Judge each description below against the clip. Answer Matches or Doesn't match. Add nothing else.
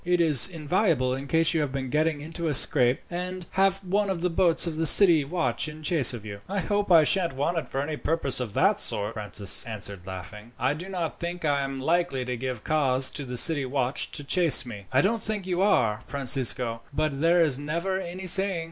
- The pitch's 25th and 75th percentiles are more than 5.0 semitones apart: Matches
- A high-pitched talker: Doesn't match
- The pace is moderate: Doesn't match